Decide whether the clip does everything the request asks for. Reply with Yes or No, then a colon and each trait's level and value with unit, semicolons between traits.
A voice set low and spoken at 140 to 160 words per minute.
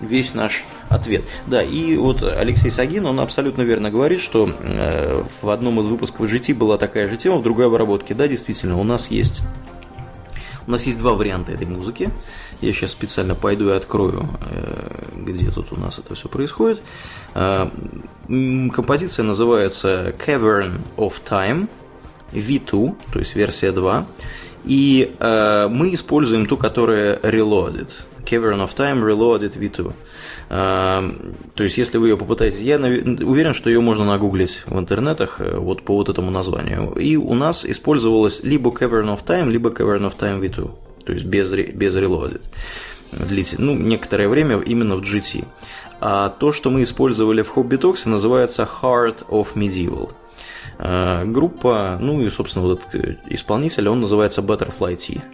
Yes: low, 110 Hz; average, 145 wpm